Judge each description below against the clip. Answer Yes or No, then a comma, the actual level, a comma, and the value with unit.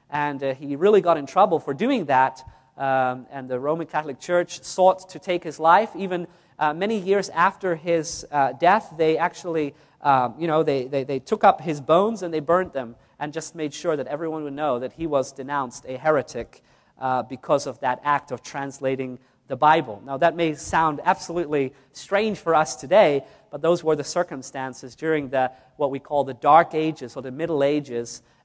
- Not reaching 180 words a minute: No, average, 200 wpm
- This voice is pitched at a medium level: Yes, medium, 150 Hz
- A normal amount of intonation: Yes, average, 4.0 semitones